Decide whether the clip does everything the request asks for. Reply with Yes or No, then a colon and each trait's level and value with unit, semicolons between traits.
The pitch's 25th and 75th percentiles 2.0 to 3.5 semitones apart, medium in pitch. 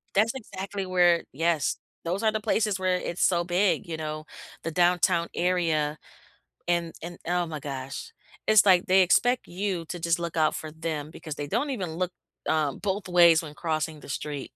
Yes: average, 2.9 semitones; medium, 170 Hz